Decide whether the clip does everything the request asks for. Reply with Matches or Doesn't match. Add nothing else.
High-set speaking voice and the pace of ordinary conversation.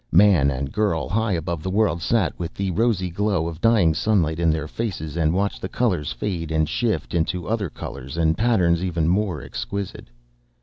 Doesn't match